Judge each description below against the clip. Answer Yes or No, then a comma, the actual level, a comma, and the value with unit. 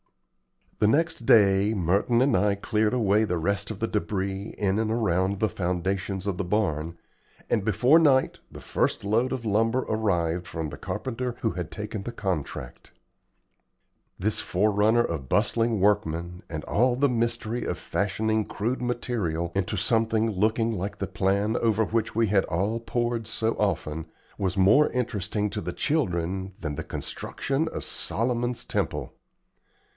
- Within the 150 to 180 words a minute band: Yes, average, 155 wpm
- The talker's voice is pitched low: Yes, low, 105 Hz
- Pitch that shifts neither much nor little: Yes, average, 3.5 semitones